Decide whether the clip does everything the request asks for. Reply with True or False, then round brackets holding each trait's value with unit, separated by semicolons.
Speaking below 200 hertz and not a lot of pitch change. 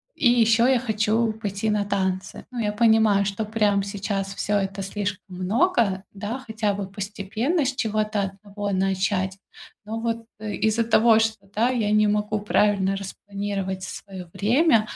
False (210 Hz; 2.1 semitones)